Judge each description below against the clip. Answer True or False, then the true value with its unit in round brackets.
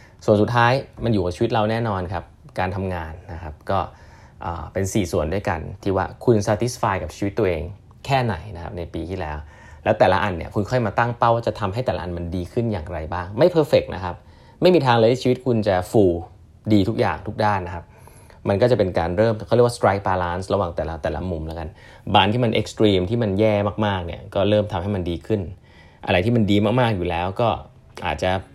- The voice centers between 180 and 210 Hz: False (100 Hz)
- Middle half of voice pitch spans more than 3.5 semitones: True (4.0 semitones)